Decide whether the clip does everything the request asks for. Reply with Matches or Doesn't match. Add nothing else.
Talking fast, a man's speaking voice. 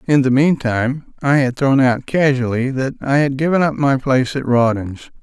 Doesn't match